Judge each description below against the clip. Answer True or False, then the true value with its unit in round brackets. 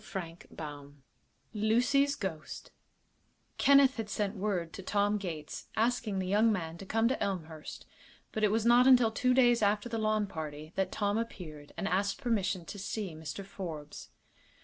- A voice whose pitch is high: True (200 Hz)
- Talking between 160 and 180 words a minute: True (165 wpm)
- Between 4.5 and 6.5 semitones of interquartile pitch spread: True (4.8 semitones)